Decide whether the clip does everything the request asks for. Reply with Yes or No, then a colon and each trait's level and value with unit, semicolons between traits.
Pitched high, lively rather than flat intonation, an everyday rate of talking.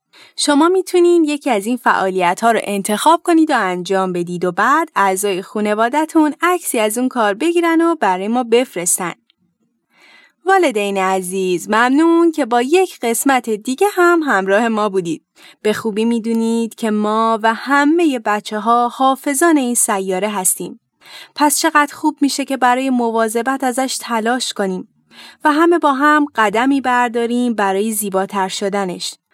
Yes: high, 240 Hz; wide, 6.3 semitones; average, 145 wpm